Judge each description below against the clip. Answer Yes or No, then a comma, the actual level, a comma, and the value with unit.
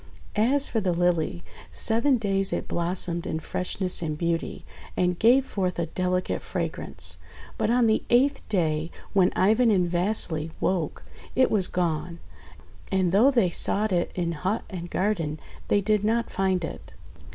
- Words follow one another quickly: No, average, 155 wpm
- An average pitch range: Yes, average, 4.1 semitones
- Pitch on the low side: No, medium, 185 Hz